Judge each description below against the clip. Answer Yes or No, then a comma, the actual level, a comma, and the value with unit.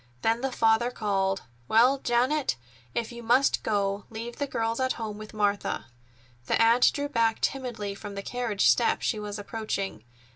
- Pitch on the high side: Yes, high, 225 Hz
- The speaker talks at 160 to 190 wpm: Yes, average, 170 wpm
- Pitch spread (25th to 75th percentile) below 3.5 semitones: Yes, average, 2.9 semitones